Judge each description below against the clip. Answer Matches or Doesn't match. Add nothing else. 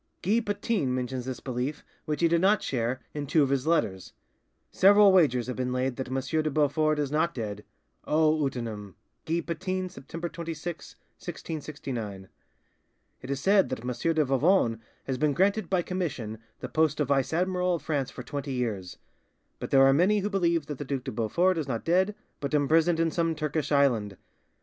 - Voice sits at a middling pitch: Matches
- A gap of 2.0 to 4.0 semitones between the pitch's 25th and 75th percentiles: Doesn't match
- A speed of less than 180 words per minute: Doesn't match